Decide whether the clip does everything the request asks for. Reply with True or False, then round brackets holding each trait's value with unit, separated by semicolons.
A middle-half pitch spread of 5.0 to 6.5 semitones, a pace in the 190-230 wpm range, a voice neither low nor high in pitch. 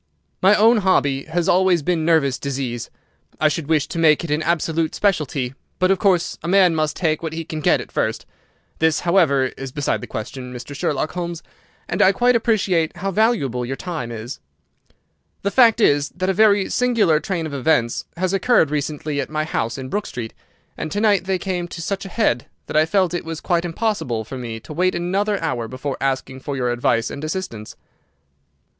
True (5.4 semitones; 200 wpm; 160 Hz)